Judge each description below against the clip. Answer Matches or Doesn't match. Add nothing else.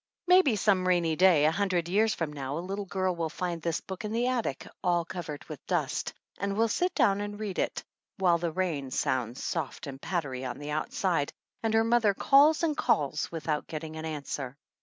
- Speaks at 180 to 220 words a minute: Matches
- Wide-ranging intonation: Doesn't match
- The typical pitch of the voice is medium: Matches